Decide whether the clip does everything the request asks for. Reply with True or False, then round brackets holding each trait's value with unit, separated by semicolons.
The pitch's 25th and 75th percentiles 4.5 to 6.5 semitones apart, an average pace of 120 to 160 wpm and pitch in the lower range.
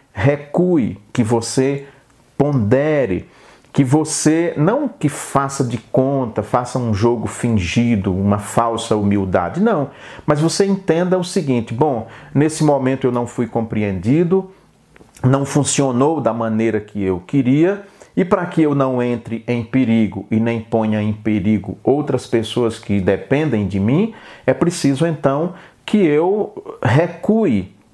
True (4.9 semitones; 135 wpm; 130 Hz)